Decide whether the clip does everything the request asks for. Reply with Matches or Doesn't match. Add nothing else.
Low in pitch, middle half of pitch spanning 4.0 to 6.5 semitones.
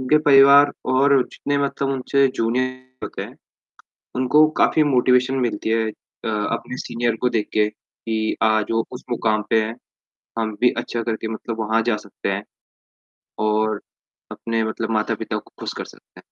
Doesn't match